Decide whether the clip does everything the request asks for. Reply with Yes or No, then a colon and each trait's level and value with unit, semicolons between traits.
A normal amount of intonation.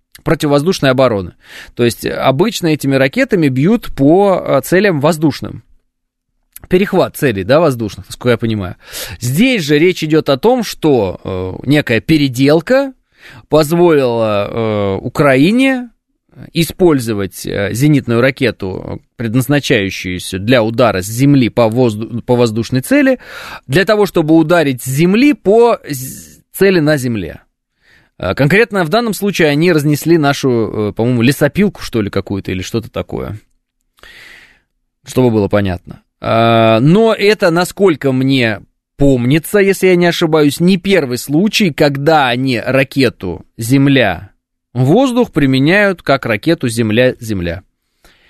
No: wide, 7.1 semitones